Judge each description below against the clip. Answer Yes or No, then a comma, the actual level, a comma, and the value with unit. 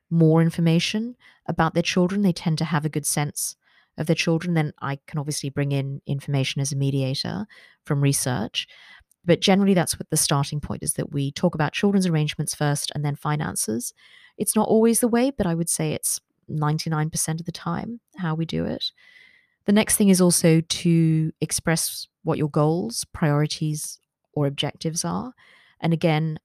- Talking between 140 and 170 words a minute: No, average, 180 wpm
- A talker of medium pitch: Yes, medium, 160 Hz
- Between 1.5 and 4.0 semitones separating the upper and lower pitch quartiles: Yes, average, 3.2 semitones